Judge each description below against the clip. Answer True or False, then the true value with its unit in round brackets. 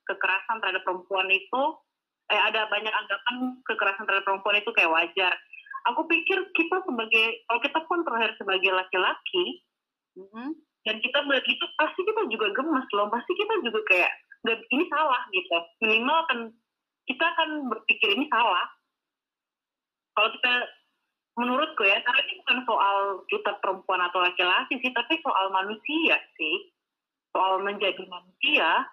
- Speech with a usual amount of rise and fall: False (8.2 semitones)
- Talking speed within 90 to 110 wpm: False (140 wpm)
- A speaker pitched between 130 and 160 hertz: False (230 Hz)